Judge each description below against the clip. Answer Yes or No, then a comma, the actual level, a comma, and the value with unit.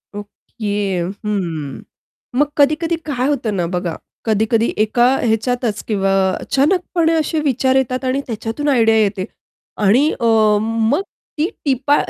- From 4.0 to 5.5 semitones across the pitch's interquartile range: Yes, average, 5.0 semitones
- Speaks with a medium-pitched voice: No, high, 235 Hz